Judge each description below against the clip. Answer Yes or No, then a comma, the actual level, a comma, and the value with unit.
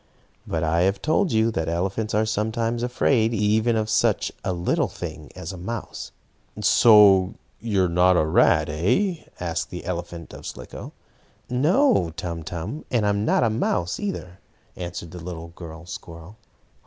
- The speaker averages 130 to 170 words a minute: Yes, average, 160 wpm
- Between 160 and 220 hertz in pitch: No, very low, 95 Hz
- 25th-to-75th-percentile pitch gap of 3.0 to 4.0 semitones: No, average, 4.6 semitones